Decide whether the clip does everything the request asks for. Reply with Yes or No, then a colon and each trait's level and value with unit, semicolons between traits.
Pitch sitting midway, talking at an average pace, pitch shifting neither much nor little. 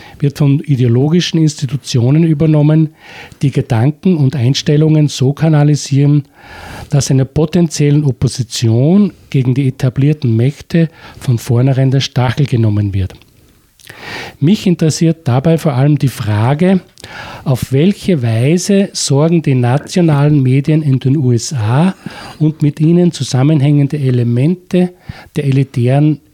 No: medium, 145 Hz; slow, 110 wpm; average, 3.4 semitones